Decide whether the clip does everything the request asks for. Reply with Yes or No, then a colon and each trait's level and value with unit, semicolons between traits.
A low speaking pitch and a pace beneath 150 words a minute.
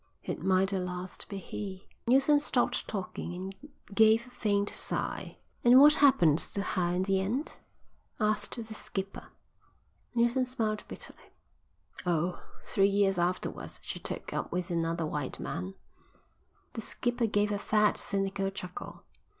No: high, 200 Hz; average, 140 wpm